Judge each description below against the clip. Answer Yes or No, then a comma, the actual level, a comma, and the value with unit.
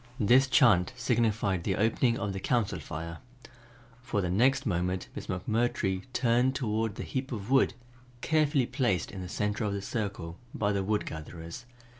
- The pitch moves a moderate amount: Yes, average, 4.6 semitones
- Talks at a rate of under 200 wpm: Yes, average, 165 wpm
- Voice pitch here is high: No, low, 105 Hz